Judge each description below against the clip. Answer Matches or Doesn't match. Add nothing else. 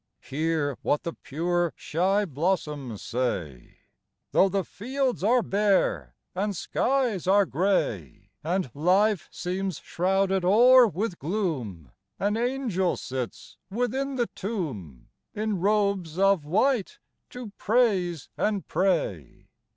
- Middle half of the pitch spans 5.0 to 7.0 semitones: Matches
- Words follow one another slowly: Matches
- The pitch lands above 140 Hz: Matches